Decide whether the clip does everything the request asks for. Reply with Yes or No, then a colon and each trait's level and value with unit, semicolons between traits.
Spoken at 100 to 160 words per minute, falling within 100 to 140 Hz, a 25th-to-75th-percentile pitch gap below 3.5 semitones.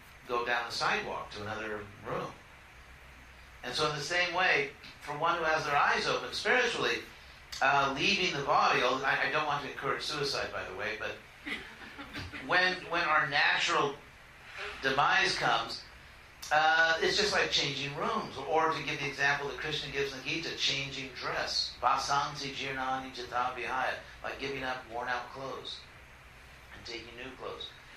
No: average, 155 wpm; low, 135 Hz; average, 3.9 semitones